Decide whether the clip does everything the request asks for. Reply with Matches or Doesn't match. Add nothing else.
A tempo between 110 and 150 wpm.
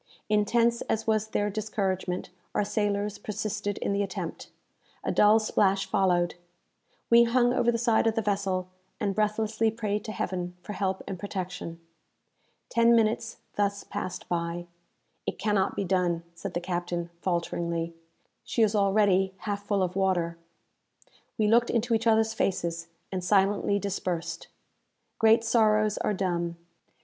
Matches